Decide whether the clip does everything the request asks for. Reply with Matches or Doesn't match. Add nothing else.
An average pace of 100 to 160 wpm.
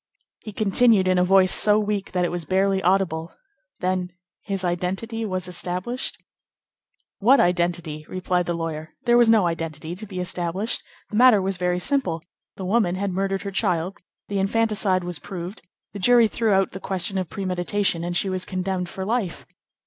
Doesn't match